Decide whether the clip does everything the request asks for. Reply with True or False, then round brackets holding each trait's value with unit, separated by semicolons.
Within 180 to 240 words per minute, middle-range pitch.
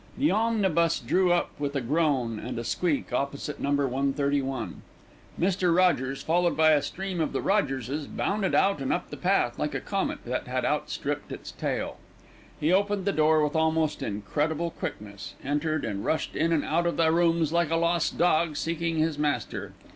True (185 wpm; 160 Hz)